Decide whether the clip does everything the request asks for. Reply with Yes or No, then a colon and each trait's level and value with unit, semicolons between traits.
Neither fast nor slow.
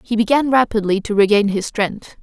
Yes: average, 190 wpm